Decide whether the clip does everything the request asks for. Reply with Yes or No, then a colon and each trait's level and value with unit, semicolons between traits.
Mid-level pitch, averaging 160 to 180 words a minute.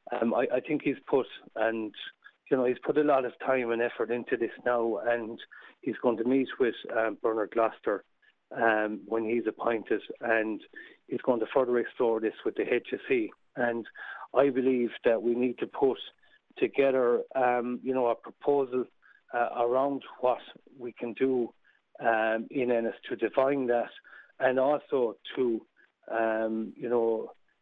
No: low, 120 Hz; average, 165 wpm